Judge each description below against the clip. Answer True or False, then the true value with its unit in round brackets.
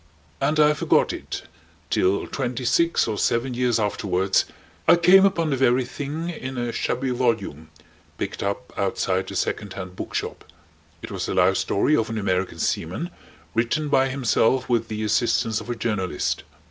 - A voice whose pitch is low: True (120 Hz)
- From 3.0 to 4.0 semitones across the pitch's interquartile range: False (4.8 semitones)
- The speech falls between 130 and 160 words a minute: False (170 wpm)